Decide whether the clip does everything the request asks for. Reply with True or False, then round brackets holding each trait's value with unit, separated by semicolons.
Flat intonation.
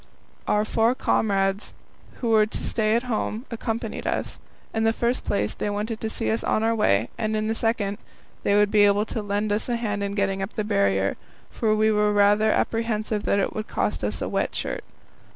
True (1.5 semitones)